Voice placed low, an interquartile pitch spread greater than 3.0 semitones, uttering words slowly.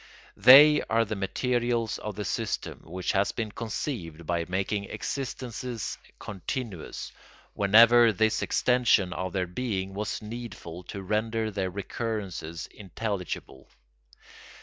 Yes: low, 105 Hz; average, 3.9 semitones; slow, 115 wpm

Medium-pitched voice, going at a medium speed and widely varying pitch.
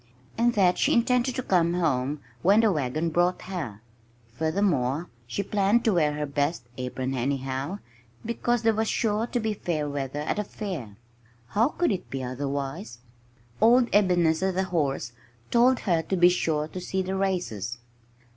Yes: medium, 175 Hz; average, 165 wpm; wide, 6.6 semitones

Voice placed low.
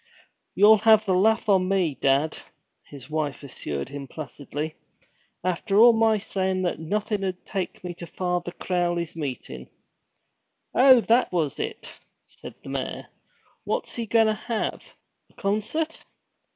No: medium, 185 Hz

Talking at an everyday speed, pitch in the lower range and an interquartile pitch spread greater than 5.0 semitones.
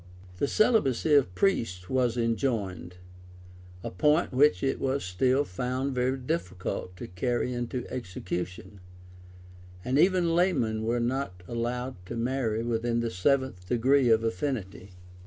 No: slow, 130 wpm; low, 120 Hz; wide, 5.5 semitones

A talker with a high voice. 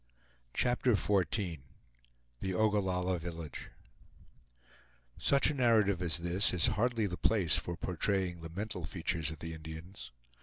No: very low, 90 Hz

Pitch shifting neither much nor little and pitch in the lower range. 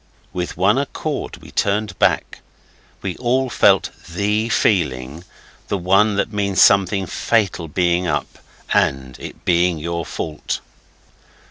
Yes: average, 3.5 semitones; very low, 95 Hz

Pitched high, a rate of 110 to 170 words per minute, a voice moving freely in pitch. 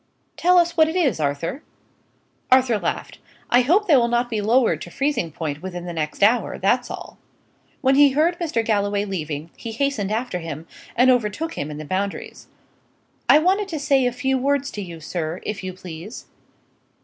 No: high, 230 Hz; average, 185 wpm; wide, 7.6 semitones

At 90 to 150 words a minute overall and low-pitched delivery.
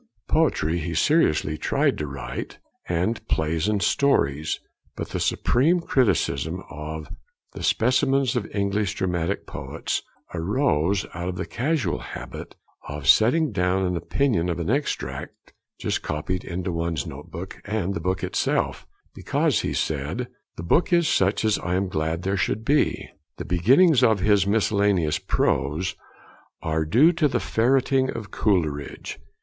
Yes: average, 145 wpm; very low, 95 Hz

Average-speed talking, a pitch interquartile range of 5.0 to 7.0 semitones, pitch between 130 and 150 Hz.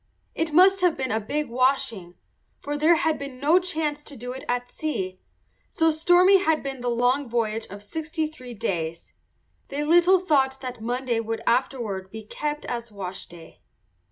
No: average, 170 wpm; wide, 5.5 semitones; very high, 265 Hz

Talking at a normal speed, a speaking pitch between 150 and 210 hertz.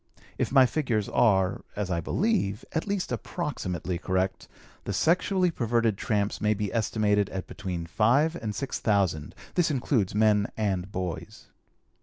No: average, 145 wpm; low, 105 Hz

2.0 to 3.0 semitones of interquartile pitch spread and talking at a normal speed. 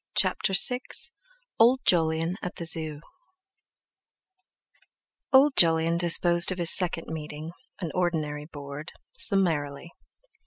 No: average, 2.7 semitones; slow, 90 wpm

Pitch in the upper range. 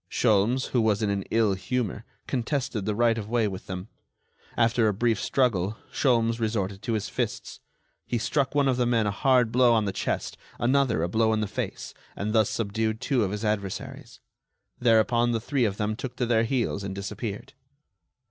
No: low, 115 Hz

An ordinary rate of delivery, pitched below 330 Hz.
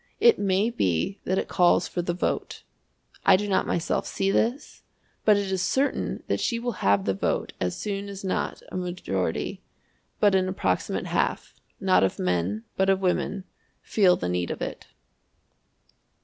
Yes: average, 170 wpm; high, 190 Hz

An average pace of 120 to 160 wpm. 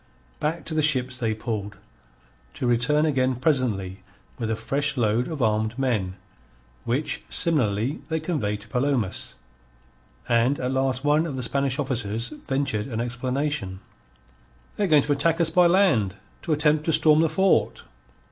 Yes: average, 155 wpm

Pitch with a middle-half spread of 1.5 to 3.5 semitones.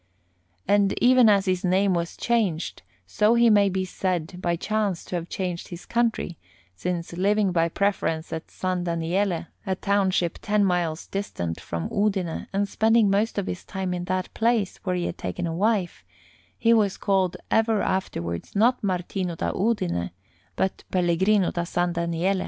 Yes: average, 2.9 semitones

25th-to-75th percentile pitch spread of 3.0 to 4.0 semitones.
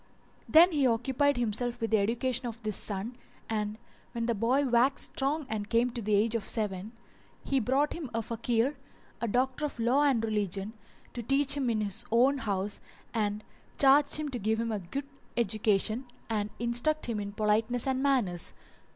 Yes: average, 3.7 semitones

